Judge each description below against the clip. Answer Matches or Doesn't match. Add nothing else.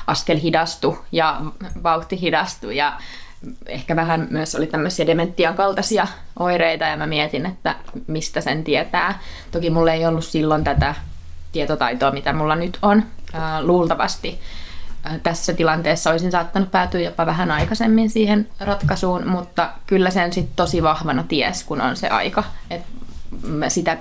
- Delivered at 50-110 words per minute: Doesn't match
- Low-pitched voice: Doesn't match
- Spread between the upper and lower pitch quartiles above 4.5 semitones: Doesn't match